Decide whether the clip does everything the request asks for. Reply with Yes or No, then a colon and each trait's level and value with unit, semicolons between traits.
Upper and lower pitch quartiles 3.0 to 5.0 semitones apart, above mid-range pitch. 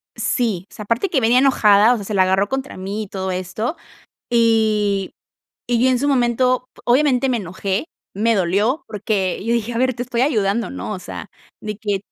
Yes: average, 3.8 semitones; high, 225 Hz